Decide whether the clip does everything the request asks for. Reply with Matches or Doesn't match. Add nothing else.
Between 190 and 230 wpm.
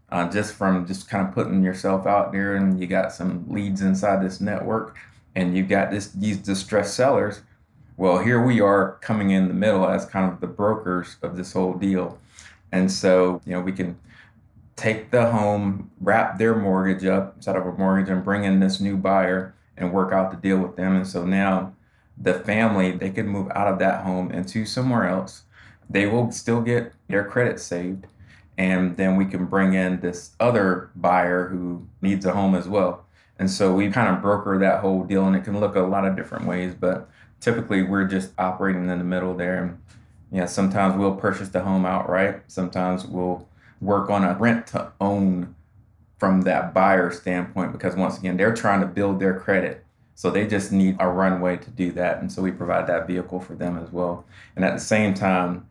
Matches